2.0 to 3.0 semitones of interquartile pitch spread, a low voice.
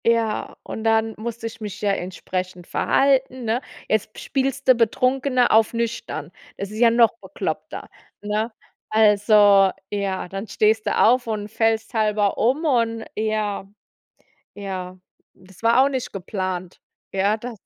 No: narrow, 2.6 semitones; high, 220 Hz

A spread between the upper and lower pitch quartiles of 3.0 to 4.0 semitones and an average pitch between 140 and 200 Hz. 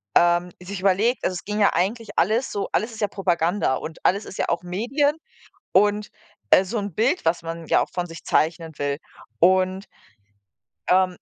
Yes: average, 3.3 semitones; medium, 185 Hz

